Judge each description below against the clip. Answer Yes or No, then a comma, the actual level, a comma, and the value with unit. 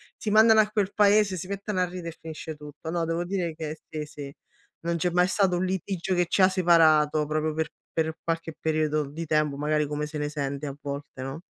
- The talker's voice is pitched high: No, medium, 160 Hz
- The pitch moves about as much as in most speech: Yes, average, 3.3 semitones